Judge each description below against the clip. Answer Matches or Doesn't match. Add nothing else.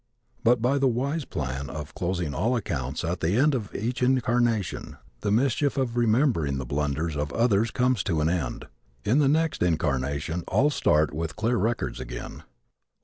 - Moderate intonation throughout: Doesn't match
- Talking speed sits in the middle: Matches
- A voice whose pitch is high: Doesn't match